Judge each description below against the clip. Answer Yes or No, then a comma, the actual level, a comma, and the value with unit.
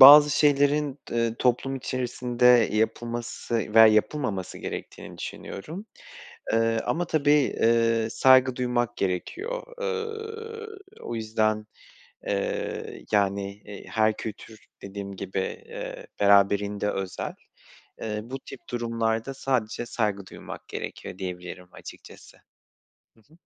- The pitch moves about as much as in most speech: Yes, average, 4.4 semitones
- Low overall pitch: Yes, low, 115 Hz